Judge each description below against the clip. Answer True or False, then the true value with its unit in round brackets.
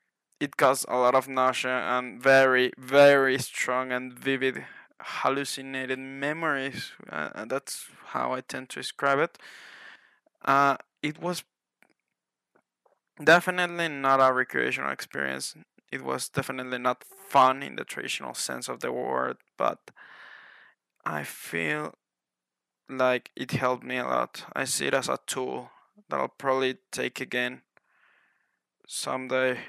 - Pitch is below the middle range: True (130 Hz)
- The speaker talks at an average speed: False (125 wpm)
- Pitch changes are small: True (1.3 semitones)